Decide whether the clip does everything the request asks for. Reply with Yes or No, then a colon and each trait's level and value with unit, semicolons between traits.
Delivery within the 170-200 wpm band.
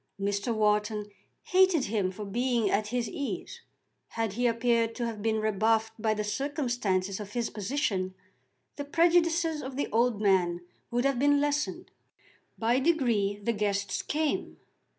No: average, 150 wpm